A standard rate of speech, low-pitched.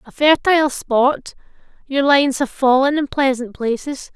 No: average, 145 wpm; very high, 270 Hz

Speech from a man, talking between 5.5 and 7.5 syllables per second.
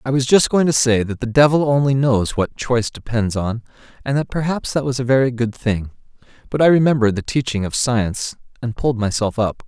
Yes: male; 5.8 syllables/s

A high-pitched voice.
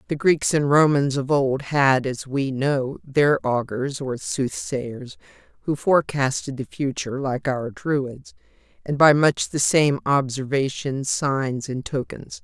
No: low, 135 Hz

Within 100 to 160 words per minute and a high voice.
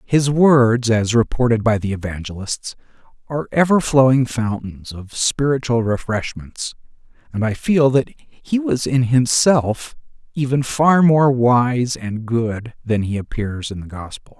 No: average, 140 wpm; low, 120 Hz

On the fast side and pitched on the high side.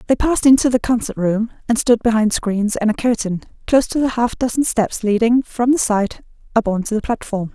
Yes: fast, 225 wpm; high, 230 Hz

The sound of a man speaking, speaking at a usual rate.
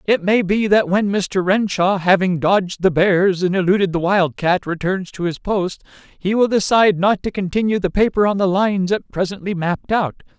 Yes: male; average, 195 wpm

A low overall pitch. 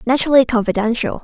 No: high, 240 Hz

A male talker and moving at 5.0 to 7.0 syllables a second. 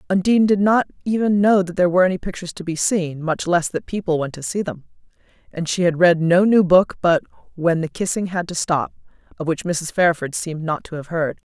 No: female; 5.9 syllables/s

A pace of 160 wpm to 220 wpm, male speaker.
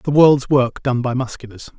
Yes: average, 200 wpm; male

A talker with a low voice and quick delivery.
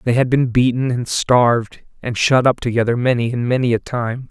Yes: low, 120 Hz; fast, 210 wpm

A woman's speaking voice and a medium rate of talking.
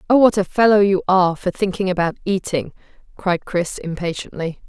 Yes: female; average, 165 wpm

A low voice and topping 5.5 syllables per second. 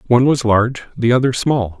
Yes: low, 120 Hz; 6.2 syllables/s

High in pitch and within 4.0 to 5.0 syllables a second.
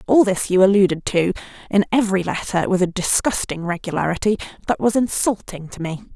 No: high, 195 Hz; 5.8 syllables/s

